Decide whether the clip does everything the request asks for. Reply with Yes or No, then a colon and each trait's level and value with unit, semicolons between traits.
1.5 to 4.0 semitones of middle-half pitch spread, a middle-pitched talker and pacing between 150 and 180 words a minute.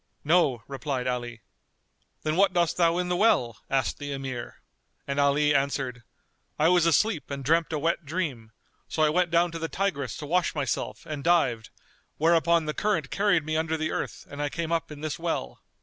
No: average, 3.5 semitones; medium, 155 Hz; average, 195 wpm